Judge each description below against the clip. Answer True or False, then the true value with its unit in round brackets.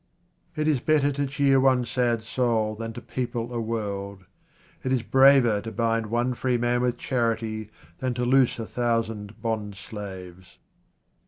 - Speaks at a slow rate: False (160 wpm)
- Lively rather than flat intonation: False (2.6 semitones)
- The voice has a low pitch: True (120 Hz)